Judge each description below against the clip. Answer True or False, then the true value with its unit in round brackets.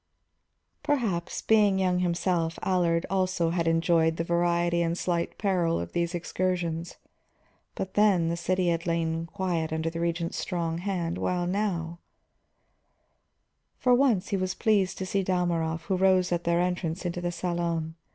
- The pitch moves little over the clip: True (1.9 semitones)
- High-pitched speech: False (175 Hz)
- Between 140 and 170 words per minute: True (150 wpm)